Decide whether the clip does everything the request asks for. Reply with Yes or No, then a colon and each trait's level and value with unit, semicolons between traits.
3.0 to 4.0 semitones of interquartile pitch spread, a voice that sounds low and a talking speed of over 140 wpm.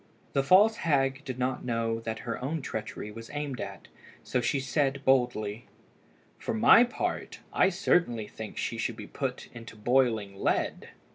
Yes: average, 3.6 semitones; low, 125 Hz; average, 160 wpm